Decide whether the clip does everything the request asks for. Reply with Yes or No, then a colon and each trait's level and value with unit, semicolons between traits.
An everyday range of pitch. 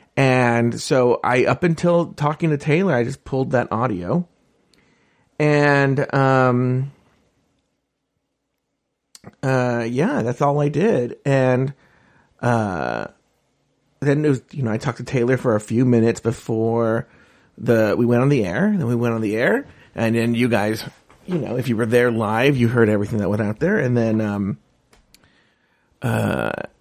Yes: average, 3.5 semitones